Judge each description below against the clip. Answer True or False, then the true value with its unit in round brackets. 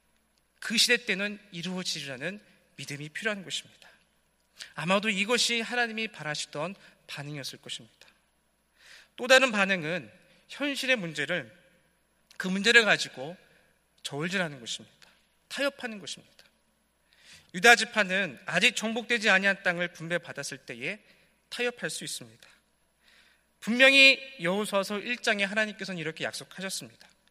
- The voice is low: False (195 Hz)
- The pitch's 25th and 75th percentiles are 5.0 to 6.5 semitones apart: True (5.5 semitones)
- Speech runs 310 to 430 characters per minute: False (295 characters per minute)